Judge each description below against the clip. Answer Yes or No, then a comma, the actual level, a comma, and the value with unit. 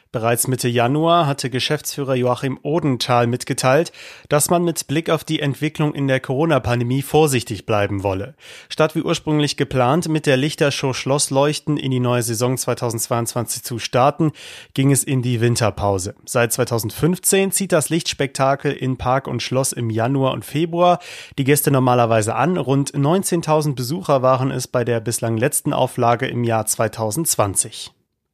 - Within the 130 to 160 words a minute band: Yes, average, 150 wpm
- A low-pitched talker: Yes, low, 130 Hz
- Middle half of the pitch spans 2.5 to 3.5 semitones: No, average, 3.9 semitones